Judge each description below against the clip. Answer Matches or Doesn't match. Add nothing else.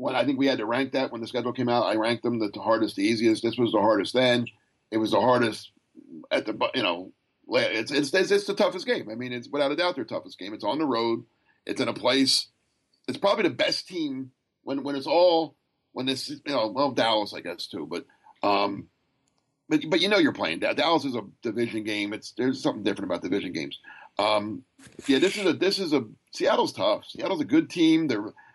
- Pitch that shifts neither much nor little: Doesn't match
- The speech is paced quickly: Matches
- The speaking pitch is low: Matches